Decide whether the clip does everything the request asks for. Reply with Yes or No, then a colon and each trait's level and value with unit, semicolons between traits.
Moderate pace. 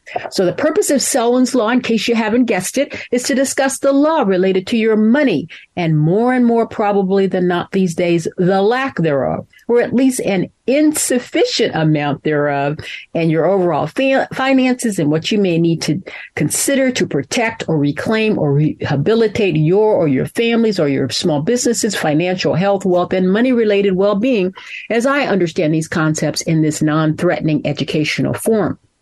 Yes: average, 170 wpm